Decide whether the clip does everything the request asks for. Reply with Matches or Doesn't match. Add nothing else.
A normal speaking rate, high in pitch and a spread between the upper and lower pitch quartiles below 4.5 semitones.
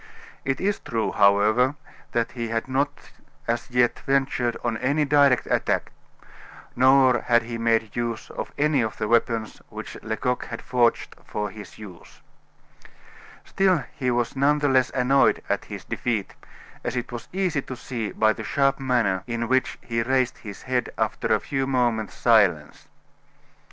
Doesn't match